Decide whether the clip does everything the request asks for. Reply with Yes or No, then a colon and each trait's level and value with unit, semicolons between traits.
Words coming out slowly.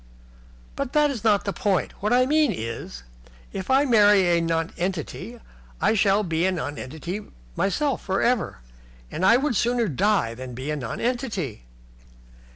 No: average, 155 wpm